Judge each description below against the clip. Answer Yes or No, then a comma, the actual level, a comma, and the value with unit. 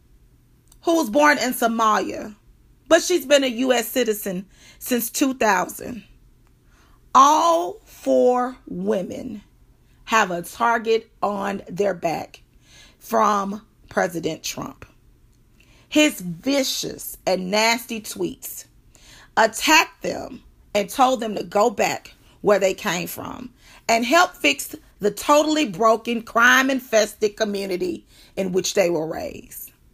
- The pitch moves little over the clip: No, average, 4.9 semitones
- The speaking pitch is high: Yes, high, 230 Hz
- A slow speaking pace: Yes, slow, 110 wpm